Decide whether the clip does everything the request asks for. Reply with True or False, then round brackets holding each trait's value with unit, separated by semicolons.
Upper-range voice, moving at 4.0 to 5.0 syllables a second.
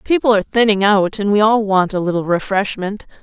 False (205 Hz; 5.7 syllables/s)